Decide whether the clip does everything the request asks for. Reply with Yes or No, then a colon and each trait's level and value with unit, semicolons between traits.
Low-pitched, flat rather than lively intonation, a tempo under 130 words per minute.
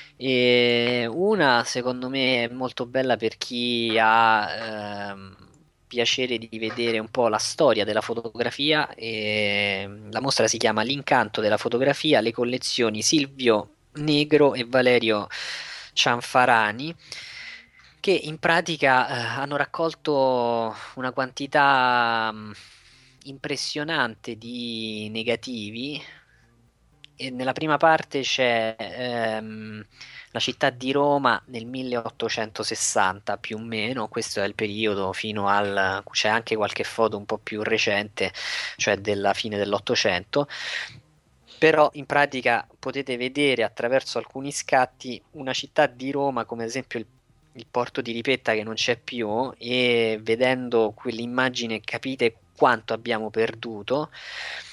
No: low, 120 Hz; average, 3.1 semitones; average, 120 wpm